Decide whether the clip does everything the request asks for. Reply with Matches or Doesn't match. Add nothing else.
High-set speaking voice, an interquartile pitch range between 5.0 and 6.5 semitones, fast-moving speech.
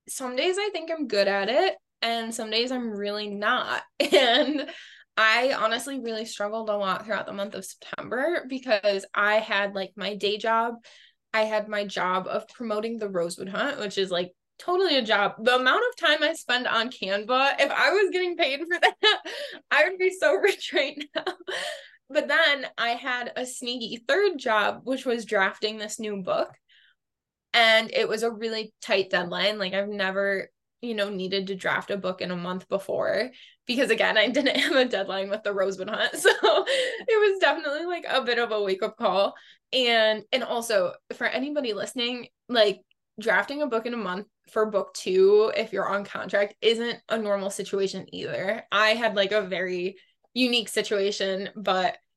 Doesn't match